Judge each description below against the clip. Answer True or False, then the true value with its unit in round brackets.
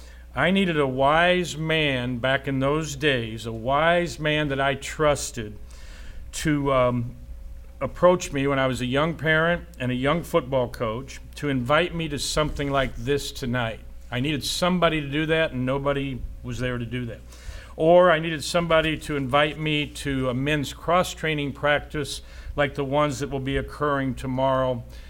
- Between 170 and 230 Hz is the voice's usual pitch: False (140 Hz)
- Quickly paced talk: False (170 wpm)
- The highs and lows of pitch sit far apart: False (3.5 semitones)